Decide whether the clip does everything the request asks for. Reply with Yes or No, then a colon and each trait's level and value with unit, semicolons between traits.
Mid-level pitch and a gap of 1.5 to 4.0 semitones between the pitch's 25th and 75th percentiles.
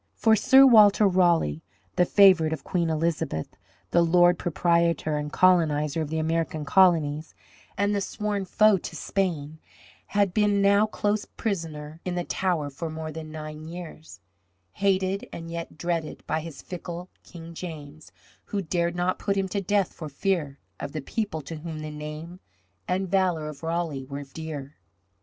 Yes: medium, 170 Hz; average, 3.4 semitones